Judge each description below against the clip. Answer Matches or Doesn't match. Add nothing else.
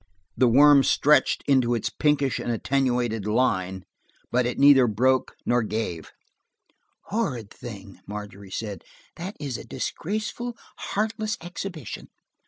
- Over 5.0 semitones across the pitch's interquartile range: Matches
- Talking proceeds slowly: Matches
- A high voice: Doesn't match